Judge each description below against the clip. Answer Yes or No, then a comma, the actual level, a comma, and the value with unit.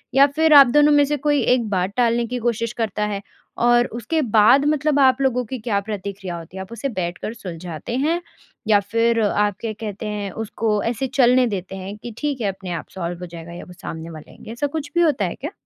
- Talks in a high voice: Yes, high, 225 Hz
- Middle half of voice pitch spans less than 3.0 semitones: No, average, 5.0 semitones